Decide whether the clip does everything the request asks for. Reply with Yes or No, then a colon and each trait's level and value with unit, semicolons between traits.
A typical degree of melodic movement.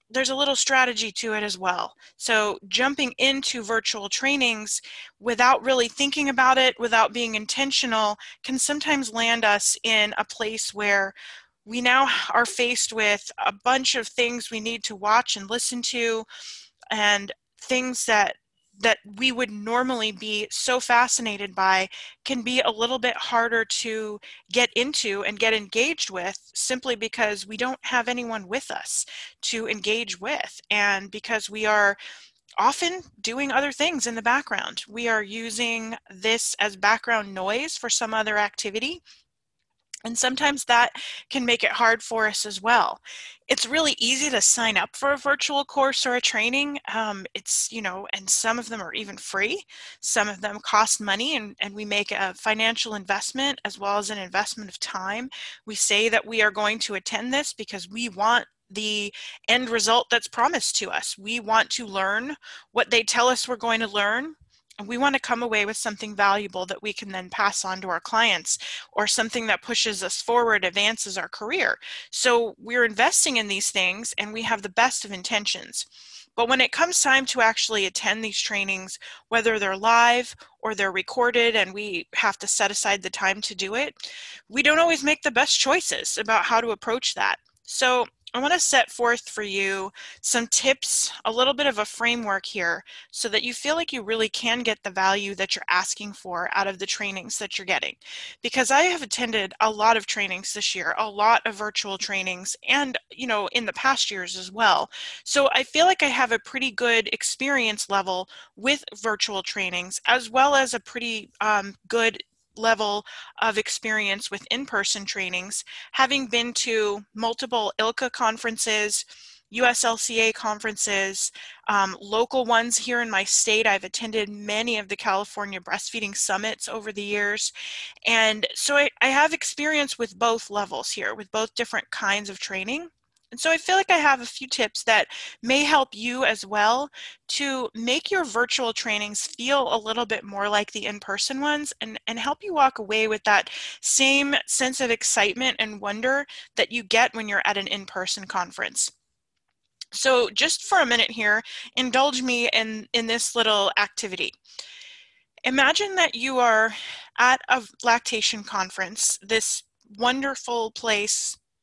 Yes: average, 3.5 semitones